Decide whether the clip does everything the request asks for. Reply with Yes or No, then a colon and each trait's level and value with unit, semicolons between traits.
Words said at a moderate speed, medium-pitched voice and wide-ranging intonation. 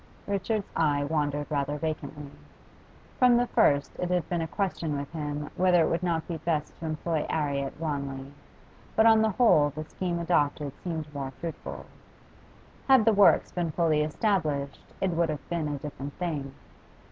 No: average, 170 wpm; medium, 155 Hz; average, 3.4 semitones